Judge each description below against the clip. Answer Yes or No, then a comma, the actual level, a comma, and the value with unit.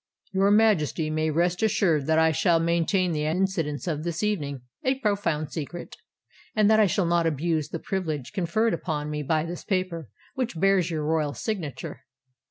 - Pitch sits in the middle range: Yes, medium, 170 Hz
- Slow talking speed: No, average, 175 wpm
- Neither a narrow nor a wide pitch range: Yes, average, 3.9 semitones